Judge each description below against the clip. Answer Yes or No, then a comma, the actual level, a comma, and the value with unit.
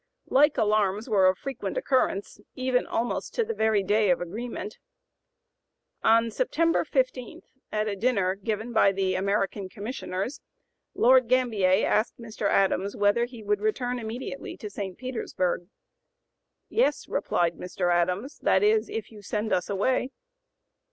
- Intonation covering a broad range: No, average, 4.1 semitones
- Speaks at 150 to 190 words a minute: No, average, 140 wpm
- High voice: Yes, high, 215 Hz